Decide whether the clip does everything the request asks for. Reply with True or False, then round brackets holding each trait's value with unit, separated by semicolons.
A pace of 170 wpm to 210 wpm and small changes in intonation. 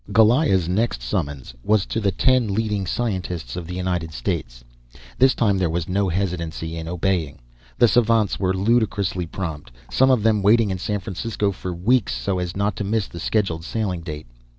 False (180 wpm; 4.1 semitones)